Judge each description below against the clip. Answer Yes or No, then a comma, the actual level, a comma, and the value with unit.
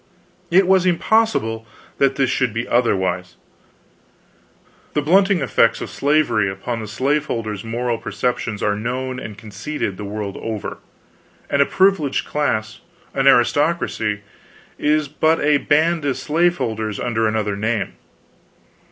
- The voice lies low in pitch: Yes, low, 125 Hz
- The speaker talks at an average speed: No, slow, 125 wpm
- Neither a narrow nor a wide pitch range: No, wide, 5.7 semitones